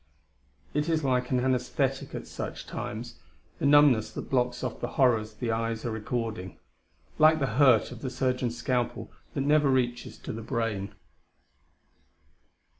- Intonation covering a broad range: No, average, 2.9 semitones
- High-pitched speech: No, low, 125 Hz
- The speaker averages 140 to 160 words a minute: Yes, average, 150 wpm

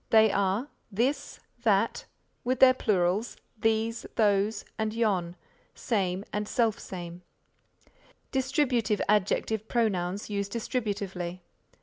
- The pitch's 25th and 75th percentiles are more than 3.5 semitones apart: No, average, 2.9 semitones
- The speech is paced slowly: Yes, slow, 95 wpm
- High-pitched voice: Yes, high, 210 Hz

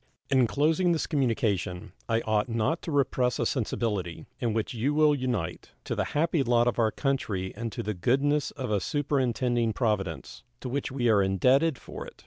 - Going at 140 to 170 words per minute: No, average, 185 wpm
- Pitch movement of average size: Yes, average, 4.4 semitones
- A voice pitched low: Yes, low, 120 Hz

